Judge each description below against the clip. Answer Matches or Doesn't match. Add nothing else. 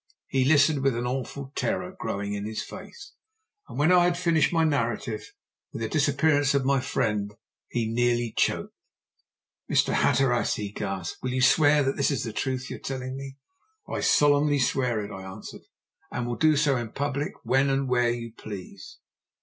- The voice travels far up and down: Doesn't match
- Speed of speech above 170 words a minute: Matches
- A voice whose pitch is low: Matches